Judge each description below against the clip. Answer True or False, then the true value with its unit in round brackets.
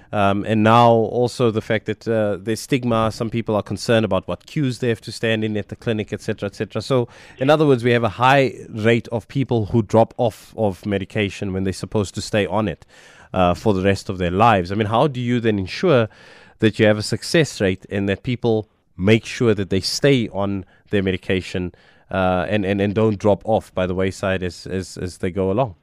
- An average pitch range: True (3.2 semitones)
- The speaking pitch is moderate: False (110 Hz)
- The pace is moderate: False (230 wpm)